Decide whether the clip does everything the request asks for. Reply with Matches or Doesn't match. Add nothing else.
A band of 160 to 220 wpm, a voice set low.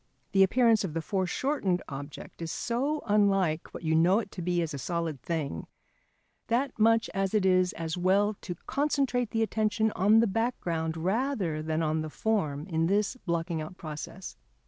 Doesn't match